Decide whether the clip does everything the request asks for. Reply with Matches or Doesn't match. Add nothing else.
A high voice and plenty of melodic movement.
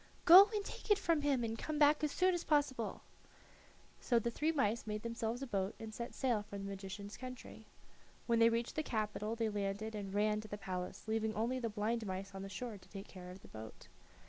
Doesn't match